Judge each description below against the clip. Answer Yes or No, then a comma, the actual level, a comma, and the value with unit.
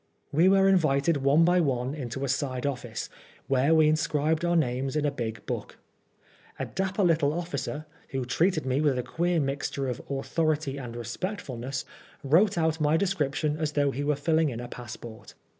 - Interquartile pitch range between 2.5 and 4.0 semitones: Yes, average, 3.6 semitones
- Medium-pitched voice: Yes, medium, 145 Hz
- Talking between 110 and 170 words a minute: No, average, 180 wpm